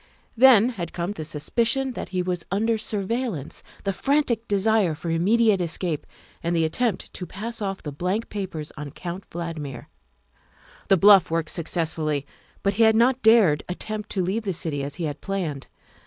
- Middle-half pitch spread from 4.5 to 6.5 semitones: Yes, average, 5.2 semitones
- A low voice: No, high, 190 Hz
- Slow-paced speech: No, average, 170 wpm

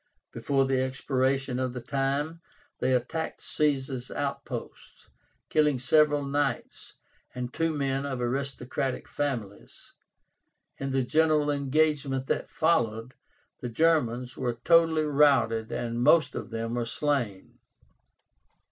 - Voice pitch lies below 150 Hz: Yes, low, 135 Hz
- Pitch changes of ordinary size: Yes, average, 3.1 semitones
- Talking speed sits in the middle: No, slow, 115 wpm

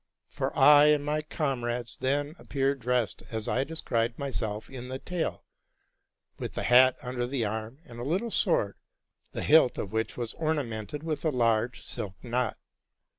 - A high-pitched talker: No, low, 125 Hz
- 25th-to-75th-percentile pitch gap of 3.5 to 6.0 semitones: Yes, average, 4.1 semitones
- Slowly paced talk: No, average, 170 wpm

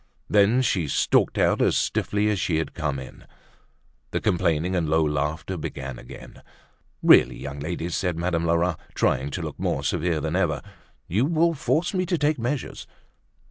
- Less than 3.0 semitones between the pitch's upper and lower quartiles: No, wide, 5.6 semitones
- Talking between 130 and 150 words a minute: No, average, 170 wpm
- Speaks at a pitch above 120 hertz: No, very low, 85 Hz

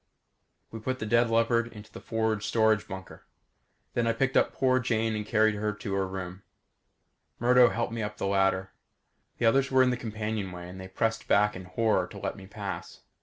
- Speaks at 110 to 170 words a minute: No, average, 200 wpm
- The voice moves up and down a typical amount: Yes, average, 3.1 semitones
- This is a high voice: No, low, 110 Hz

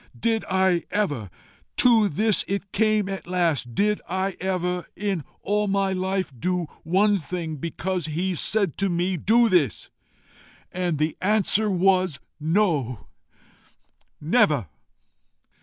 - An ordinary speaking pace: No, slow, 125 wpm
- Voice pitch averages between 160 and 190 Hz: Yes, medium, 185 Hz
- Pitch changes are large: No, average, 3.2 semitones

